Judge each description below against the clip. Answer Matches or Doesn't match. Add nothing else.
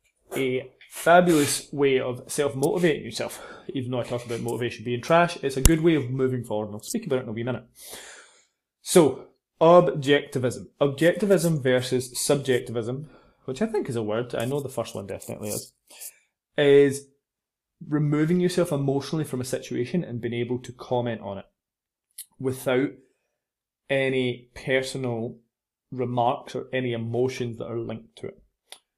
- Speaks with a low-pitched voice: Matches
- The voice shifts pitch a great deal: Doesn't match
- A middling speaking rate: Matches